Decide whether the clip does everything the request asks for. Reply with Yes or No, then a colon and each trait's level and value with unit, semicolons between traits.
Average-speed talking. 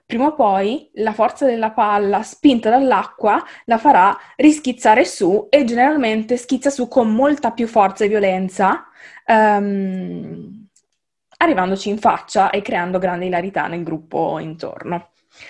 Yes: average, 130 wpm